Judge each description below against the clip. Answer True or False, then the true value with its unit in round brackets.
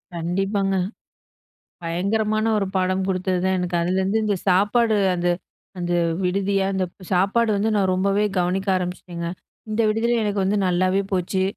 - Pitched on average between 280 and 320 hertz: False (190 Hz)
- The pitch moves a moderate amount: False (2.2 semitones)